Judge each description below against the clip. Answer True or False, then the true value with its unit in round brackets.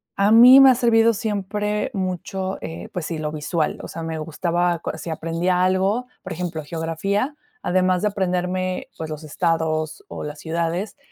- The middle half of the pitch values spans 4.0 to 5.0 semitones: False (3.6 semitones)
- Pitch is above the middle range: False (180 Hz)